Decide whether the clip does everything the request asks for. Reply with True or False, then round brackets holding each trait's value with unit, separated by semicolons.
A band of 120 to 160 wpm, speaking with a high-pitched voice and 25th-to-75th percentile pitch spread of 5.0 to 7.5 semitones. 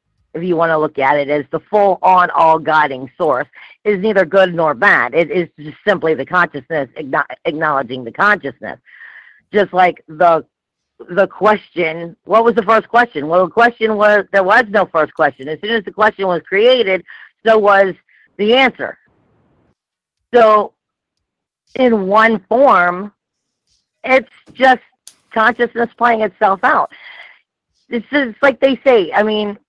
True (150 wpm; 195 Hz; 5.4 semitones)